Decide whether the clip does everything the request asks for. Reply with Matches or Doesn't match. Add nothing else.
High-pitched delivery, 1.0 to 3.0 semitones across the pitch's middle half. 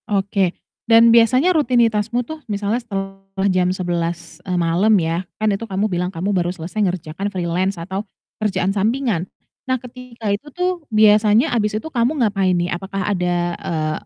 Doesn't match